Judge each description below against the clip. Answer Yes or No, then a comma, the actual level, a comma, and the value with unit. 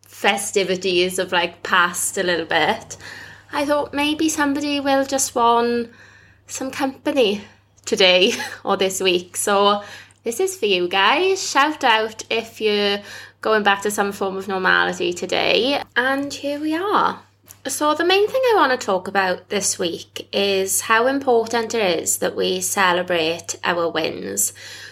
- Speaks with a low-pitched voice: No, high, 220 Hz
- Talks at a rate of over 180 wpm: No, average, 150 wpm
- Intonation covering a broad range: Yes, wide, 7.0 semitones